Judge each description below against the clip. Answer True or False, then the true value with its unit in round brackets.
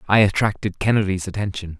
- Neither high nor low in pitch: False (100 Hz)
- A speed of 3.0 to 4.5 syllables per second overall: False (6.2 syllables/s)